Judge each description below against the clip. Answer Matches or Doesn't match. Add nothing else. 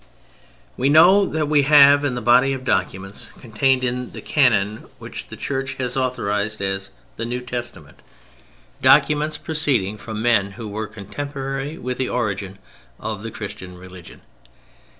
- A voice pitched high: Doesn't match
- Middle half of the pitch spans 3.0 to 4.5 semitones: Doesn't match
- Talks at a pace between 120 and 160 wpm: Matches